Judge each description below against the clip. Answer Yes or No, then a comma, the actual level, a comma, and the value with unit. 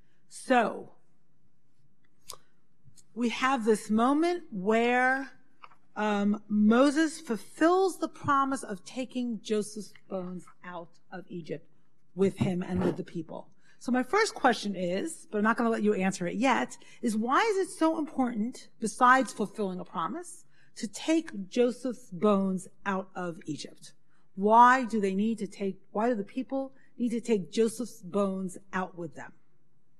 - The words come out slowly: No, average, 150 wpm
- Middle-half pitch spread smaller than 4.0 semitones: No, wide, 5.4 semitones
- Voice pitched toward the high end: Yes, high, 215 Hz